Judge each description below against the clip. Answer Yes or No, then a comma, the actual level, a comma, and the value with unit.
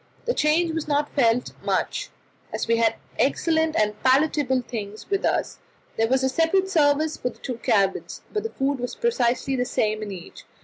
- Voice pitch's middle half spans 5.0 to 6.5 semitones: Yes, wide, 5.5 semitones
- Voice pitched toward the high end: Yes, very high, 265 Hz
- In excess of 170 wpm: Yes, average, 185 wpm